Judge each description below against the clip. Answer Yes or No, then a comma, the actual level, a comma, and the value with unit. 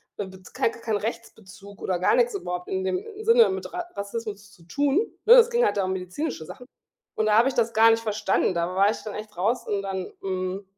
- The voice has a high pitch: Yes, high, 210 Hz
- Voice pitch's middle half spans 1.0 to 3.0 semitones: No, average, 4.8 semitones